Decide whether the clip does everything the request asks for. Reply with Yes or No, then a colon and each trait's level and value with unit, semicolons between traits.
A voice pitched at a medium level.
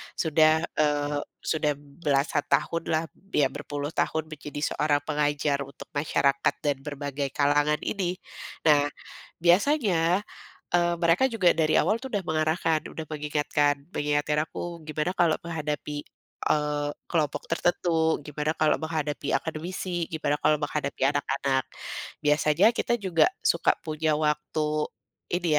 Yes: medium, 155 Hz